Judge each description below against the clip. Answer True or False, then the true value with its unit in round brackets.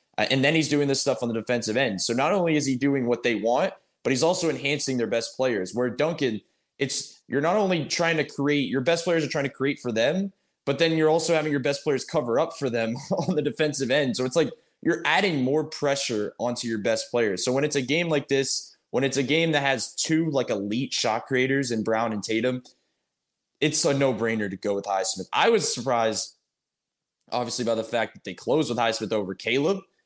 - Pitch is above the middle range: False (135 Hz)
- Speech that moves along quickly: True (230 wpm)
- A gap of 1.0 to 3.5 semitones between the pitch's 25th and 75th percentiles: False (4.5 semitones)